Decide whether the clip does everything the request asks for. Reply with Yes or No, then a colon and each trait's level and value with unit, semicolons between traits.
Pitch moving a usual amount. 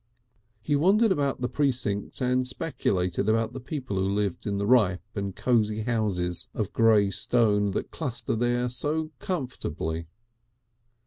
Yes: average, 4.2 semitones